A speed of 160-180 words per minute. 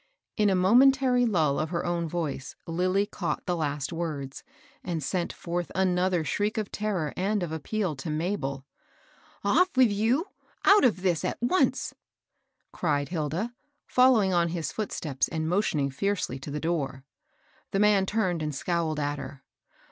Yes: average, 165 wpm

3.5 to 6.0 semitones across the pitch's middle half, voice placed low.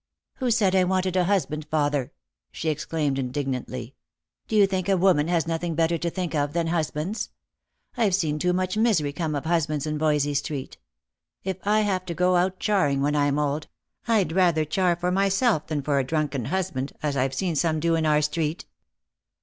No: average, 3.9 semitones; medium, 165 Hz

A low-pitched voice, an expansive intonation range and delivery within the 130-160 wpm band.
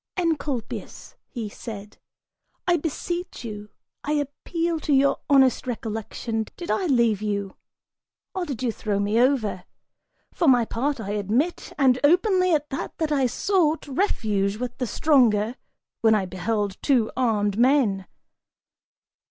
No: very high, 250 Hz; wide, 5.8 semitones; slow, 135 wpm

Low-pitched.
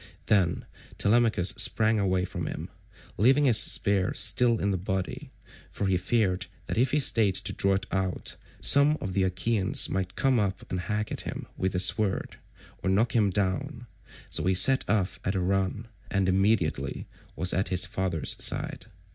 Yes: very low, 95 Hz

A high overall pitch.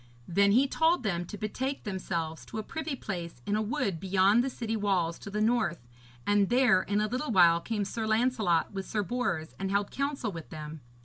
Yes: high, 205 Hz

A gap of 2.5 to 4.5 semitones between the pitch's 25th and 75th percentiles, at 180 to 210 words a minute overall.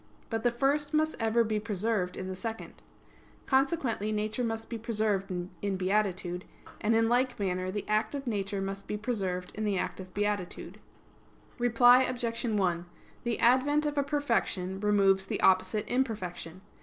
No: average, 3.9 semitones; average, 160 wpm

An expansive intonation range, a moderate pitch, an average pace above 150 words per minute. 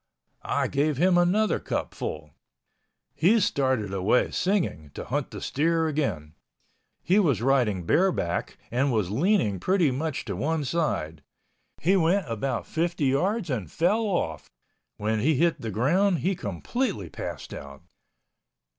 No: wide, 8.6 semitones; medium, 145 Hz; slow, 135 wpm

